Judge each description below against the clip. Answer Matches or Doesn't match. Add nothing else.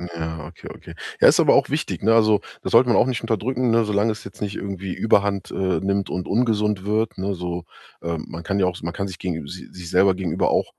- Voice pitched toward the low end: Matches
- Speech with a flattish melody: Doesn't match